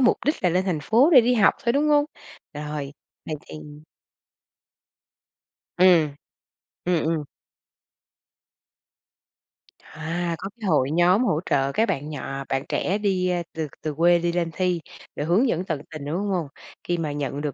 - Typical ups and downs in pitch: Yes, average, 4.0 semitones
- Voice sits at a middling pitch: Yes, medium, 170 Hz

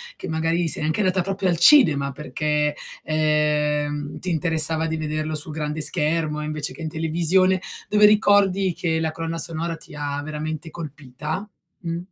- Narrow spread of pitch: Yes, narrow, 2.1 semitones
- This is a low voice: No, medium, 160 Hz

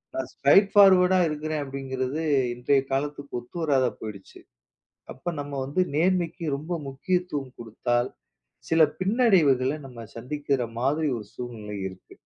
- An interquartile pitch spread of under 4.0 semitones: No, average, 4.4 semitones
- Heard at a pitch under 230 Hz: Yes, medium, 140 Hz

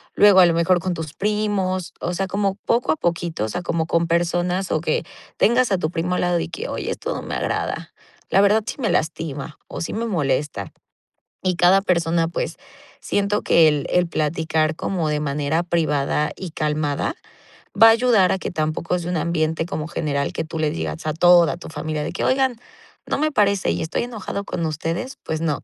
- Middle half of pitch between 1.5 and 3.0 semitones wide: No, average, 3.6 semitones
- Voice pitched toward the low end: No, medium, 170 Hz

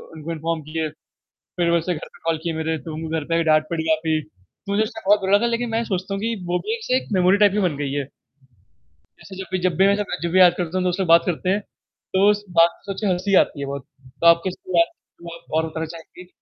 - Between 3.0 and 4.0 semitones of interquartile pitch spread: Yes, average, 3.6 semitones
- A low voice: No, medium, 175 Hz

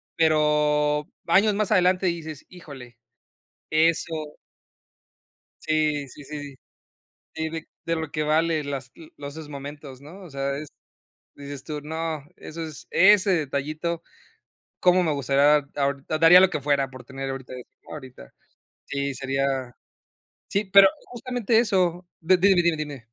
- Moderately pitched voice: Yes, medium, 150 Hz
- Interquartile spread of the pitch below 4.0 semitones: Yes, average, 3.3 semitones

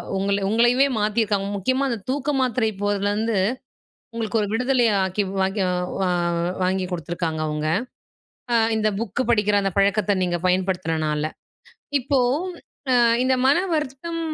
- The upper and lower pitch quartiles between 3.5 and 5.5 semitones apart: Yes, average, 4.6 semitones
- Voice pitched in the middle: No, high, 210 Hz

